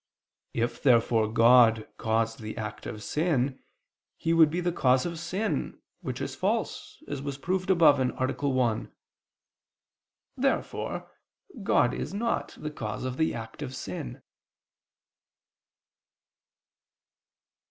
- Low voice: Yes, low, 130 Hz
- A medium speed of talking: No, slow, 120 wpm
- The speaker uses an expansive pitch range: Yes, wide, 5.9 semitones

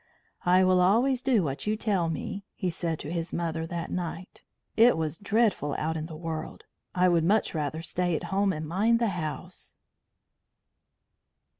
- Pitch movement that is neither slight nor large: Yes, average, 3.8 semitones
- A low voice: No, medium, 175 Hz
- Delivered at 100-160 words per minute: No, average, 170 wpm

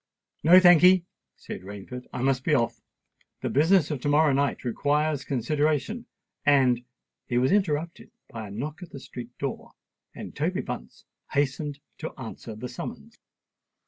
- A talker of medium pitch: Yes, medium, 145 Hz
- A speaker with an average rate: Yes, average, 150 wpm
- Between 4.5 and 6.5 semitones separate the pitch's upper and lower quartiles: No, average, 3.8 semitones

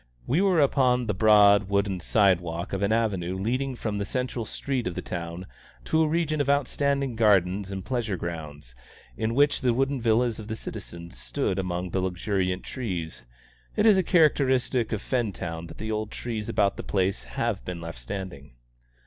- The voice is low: Yes, low, 105 Hz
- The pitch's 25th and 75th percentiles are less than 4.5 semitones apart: No, wide, 5.6 semitones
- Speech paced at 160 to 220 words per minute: Yes, average, 180 wpm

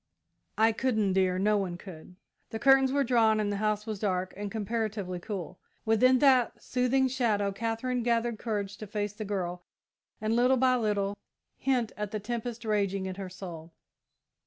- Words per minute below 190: Yes, average, 170 wpm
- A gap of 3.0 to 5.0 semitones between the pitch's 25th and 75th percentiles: Yes, average, 3.3 semitones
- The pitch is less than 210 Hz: No, high, 215 Hz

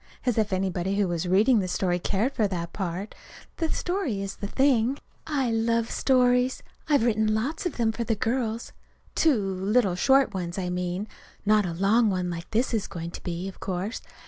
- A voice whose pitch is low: No, high, 210 Hz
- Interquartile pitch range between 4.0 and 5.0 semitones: Yes, average, 4.6 semitones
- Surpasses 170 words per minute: Yes, average, 190 wpm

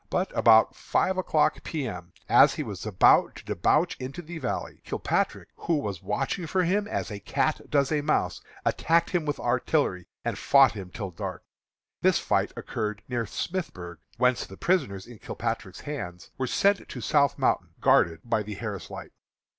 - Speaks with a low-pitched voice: Yes, low, 130 Hz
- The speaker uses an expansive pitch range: Yes, wide, 8.0 semitones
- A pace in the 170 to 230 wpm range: Yes, average, 175 wpm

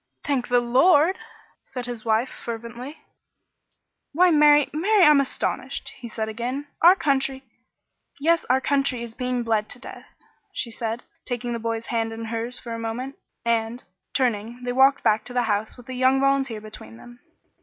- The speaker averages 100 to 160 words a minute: No, average, 175 wpm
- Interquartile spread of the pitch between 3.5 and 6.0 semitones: No, average, 3.1 semitones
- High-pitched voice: Yes, high, 245 Hz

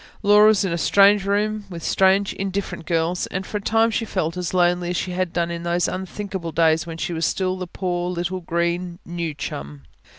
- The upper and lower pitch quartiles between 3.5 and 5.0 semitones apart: No, narrow, 2.4 semitones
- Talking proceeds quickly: Yes, fast, 210 wpm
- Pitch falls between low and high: Yes, medium, 180 Hz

